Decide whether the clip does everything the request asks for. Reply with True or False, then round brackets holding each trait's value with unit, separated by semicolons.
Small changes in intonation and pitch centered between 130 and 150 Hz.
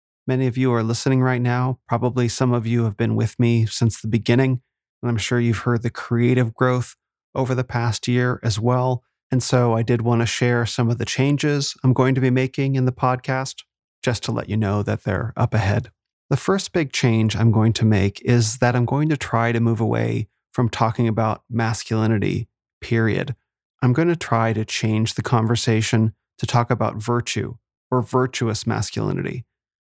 False (2.1 semitones; 120 Hz)